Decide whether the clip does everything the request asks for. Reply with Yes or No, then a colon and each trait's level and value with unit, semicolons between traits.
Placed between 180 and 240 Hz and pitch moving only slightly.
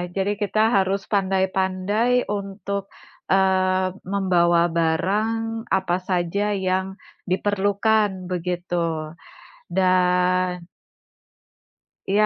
Yes: high, 190 Hz; narrow, 1.7 semitones